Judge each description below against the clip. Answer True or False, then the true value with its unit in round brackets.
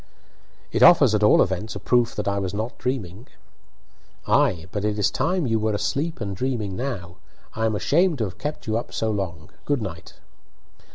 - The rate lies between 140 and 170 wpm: False (190 wpm)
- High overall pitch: False (110 Hz)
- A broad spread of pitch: False (4.5 semitones)